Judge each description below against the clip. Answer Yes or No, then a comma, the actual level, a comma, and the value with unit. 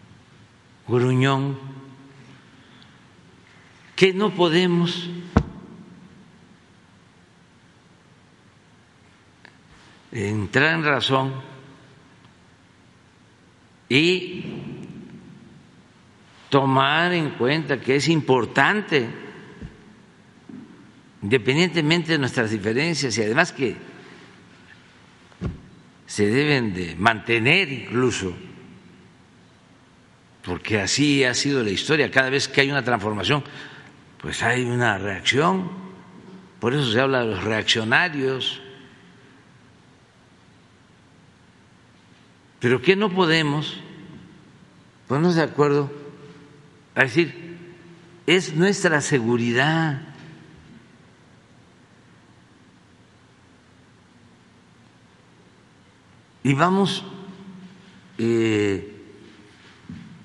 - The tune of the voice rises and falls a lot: Yes, wide, 6.0 semitones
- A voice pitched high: No, medium, 140 Hz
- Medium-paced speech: No, slow, 65 wpm